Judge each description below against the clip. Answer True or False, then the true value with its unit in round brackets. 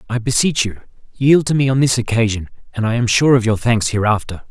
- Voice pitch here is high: False (120 Hz)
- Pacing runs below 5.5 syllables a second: False (5.9 syllables/s)